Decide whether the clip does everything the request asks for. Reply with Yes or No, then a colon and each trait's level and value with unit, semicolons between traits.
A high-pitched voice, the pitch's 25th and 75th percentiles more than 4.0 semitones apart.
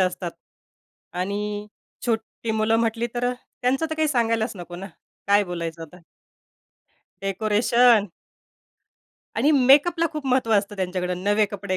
Yes: high, 215 Hz; average, 4.4 semitones